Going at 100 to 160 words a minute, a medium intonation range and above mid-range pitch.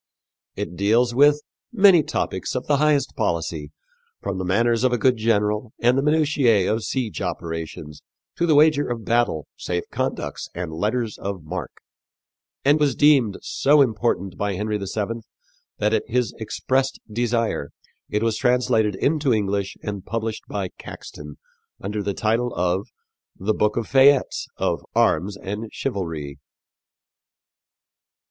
No: average, 140 wpm; average, 4.6 semitones; low, 110 Hz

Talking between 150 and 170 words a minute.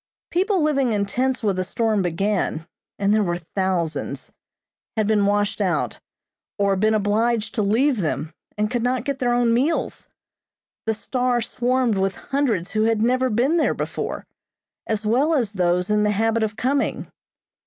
Yes: average, 165 wpm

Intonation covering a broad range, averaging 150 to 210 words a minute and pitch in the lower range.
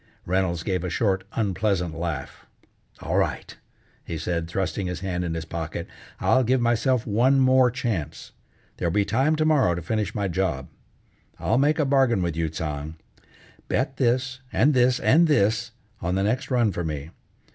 Yes: wide, 6.9 semitones; average, 170 wpm; low, 100 Hz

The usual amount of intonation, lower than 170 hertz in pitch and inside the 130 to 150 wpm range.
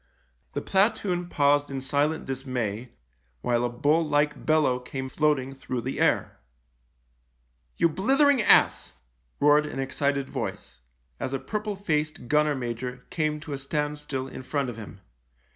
Yes: average, 3.3 semitones; medium, 140 Hz; average, 145 wpm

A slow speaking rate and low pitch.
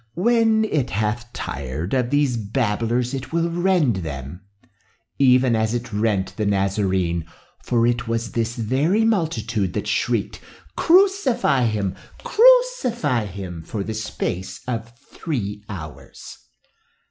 Yes: slow, 125 wpm; low, 115 Hz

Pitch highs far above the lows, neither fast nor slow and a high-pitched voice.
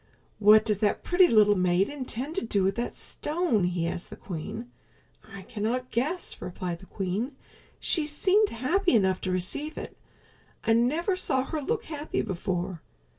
Yes: wide, 7.8 semitones; average, 165 wpm; high, 225 Hz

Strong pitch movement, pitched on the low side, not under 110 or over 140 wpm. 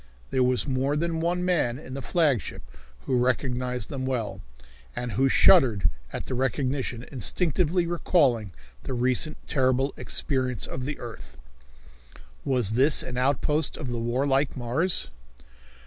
No: average, 3.1 semitones; low, 130 Hz; slow, 135 wpm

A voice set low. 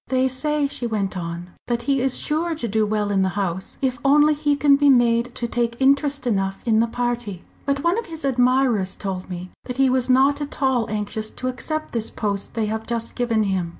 No: high, 240 Hz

